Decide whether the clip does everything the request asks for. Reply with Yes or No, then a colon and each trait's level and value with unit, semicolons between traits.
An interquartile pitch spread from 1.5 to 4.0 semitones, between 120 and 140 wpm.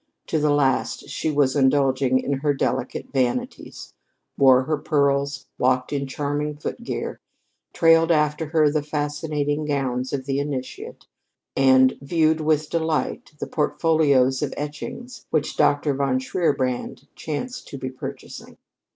Yes: narrow, 2.4 semitones; slow, 135 wpm